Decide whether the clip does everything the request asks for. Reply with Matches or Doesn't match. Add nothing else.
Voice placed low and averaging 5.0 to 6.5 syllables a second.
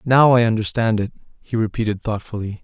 Matches